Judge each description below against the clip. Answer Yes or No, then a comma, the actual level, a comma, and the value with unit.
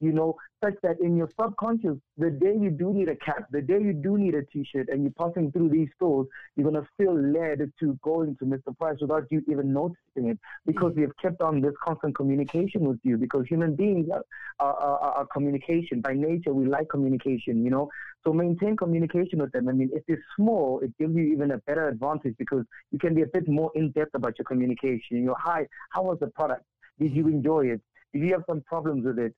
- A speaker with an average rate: No, fast, 235 wpm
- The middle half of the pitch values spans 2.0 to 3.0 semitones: No, average, 3.4 semitones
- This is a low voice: No, medium, 155 Hz